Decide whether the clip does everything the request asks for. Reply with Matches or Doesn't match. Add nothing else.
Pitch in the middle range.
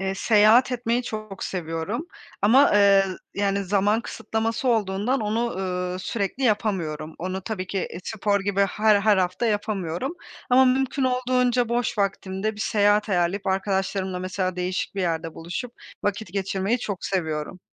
Doesn't match